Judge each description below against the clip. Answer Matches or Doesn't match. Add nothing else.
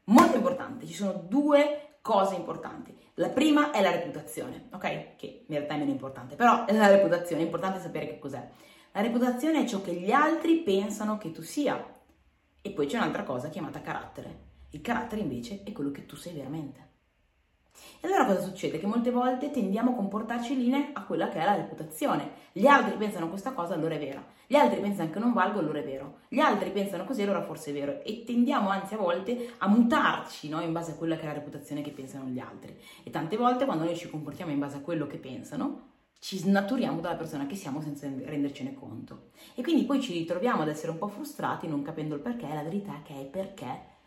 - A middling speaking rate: Doesn't match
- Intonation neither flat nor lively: Doesn't match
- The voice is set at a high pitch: Matches